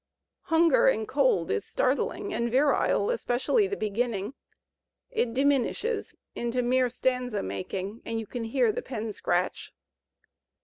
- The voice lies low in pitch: No, very high, 250 Hz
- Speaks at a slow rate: Yes, slow, 130 wpm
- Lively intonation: No, average, 4.6 semitones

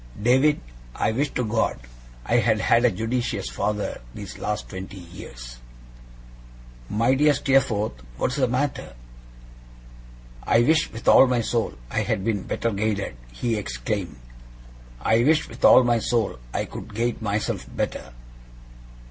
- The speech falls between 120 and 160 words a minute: Yes, average, 145 wpm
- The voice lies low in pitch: Yes, low, 115 Hz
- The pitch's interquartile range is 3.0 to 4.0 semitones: Yes, average, 3.6 semitones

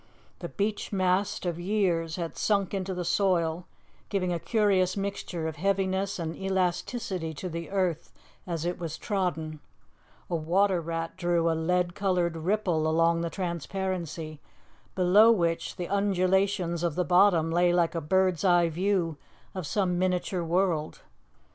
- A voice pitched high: No, medium, 180 Hz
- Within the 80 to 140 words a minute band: No, average, 150 wpm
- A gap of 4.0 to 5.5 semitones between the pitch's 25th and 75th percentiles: No, narrow, 2.4 semitones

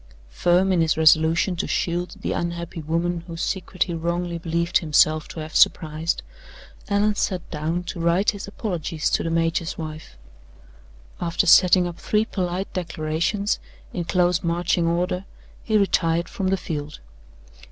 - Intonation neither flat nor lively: No, narrow, 1.9 semitones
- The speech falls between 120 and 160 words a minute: Yes, average, 150 wpm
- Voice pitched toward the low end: No, medium, 170 Hz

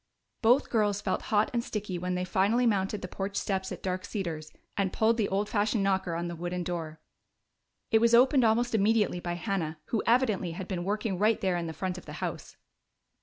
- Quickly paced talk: Yes, fast, 210 wpm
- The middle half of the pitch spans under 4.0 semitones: Yes, average, 3.6 semitones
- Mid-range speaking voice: No, high, 195 Hz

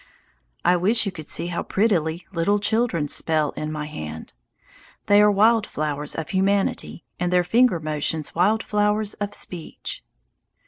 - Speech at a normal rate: Yes, average, 150 wpm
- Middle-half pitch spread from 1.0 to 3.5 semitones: No, average, 4.9 semitones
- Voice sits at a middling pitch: Yes, medium, 180 Hz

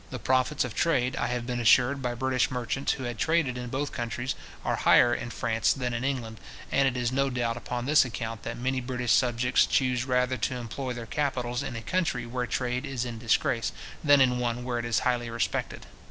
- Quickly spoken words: Yes, fast, 215 wpm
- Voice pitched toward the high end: No, low, 125 Hz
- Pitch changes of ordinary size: No, narrow, 1.6 semitones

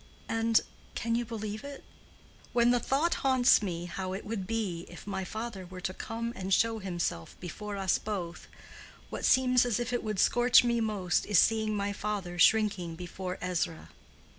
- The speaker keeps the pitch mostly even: No, average, 4.0 semitones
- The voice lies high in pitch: Yes, high, 210 Hz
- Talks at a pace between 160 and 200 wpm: Yes, average, 170 wpm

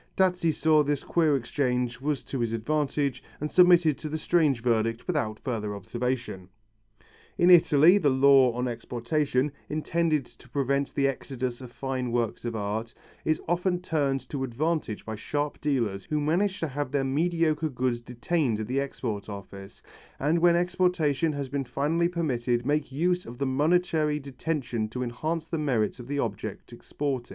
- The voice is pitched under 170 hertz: Yes, medium, 140 Hz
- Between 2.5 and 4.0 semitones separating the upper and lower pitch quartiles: No, average, 4.4 semitones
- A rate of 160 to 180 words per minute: Yes, average, 165 wpm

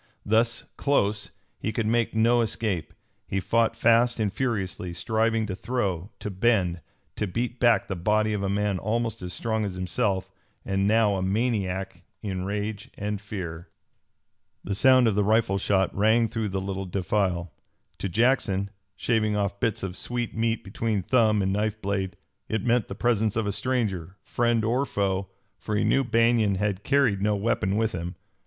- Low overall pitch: Yes, low, 105 Hz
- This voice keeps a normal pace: Yes, average, 175 wpm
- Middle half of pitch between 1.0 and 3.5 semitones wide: Yes, average, 2.9 semitones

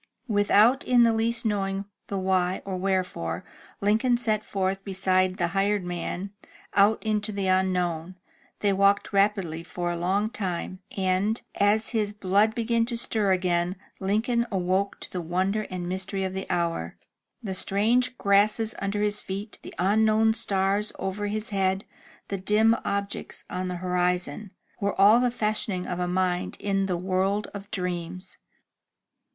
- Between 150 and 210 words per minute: Yes, average, 155 wpm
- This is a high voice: Yes, high, 195 Hz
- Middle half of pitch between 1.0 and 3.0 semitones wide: Yes, narrow, 2.4 semitones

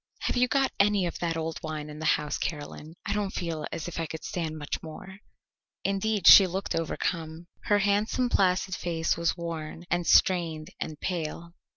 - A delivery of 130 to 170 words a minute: No, average, 185 wpm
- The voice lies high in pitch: No, medium, 170 Hz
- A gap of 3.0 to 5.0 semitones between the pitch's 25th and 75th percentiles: Yes, average, 3.4 semitones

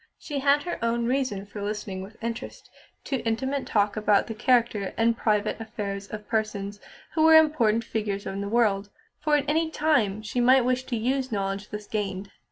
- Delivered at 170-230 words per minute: Yes, average, 185 wpm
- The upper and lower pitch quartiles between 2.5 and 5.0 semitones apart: Yes, average, 4.1 semitones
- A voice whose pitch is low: No, high, 225 Hz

